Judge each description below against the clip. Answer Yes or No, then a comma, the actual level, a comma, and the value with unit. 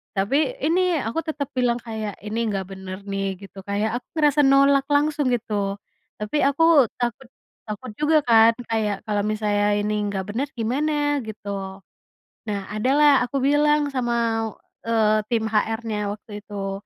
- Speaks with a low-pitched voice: No, high, 225 Hz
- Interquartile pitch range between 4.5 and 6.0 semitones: Yes, average, 5.1 semitones